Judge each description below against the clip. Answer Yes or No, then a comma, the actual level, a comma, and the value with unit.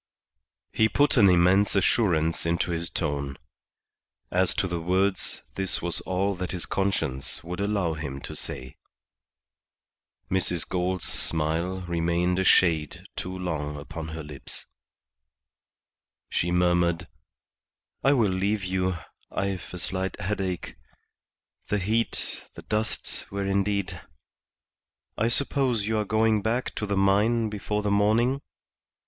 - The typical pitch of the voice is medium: No, very low, 95 Hz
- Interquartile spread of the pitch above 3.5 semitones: No, average, 3.2 semitones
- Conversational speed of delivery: No, slow, 130 wpm